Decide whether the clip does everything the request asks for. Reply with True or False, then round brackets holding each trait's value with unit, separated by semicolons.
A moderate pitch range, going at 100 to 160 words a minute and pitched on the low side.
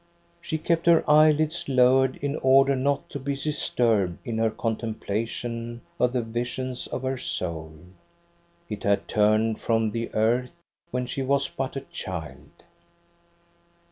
True (3.5 semitones; 140 wpm; 125 Hz)